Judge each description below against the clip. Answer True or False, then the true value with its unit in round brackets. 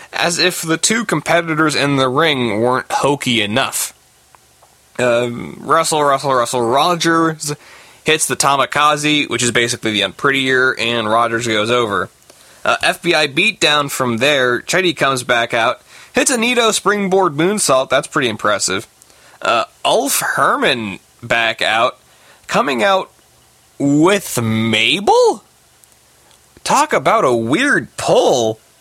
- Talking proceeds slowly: True (125 wpm)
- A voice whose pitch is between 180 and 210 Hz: False (140 Hz)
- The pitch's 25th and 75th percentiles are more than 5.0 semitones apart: True (5.5 semitones)